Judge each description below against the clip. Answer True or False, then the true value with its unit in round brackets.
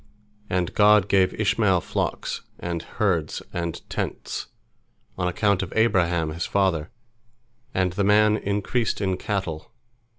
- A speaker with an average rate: False (125 wpm)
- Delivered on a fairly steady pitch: False (3.1 semitones)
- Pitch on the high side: False (95 Hz)